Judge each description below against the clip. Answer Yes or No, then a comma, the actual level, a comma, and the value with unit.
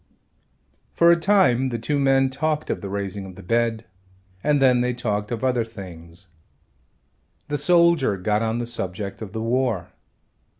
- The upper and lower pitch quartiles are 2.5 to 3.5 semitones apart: No, average, 4.9 semitones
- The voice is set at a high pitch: No, low, 120 Hz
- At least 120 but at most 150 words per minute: No, average, 165 wpm